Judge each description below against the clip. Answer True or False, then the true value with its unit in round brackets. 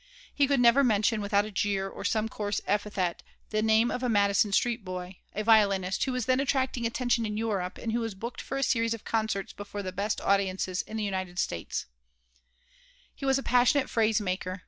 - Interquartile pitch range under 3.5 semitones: True (3.1 semitones)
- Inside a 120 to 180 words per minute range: False (205 wpm)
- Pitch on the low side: False (215 Hz)